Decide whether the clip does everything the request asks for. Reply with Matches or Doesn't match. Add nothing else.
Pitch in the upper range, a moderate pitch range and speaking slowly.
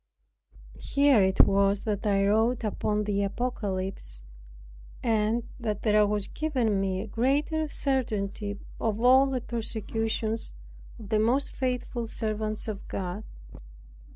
Matches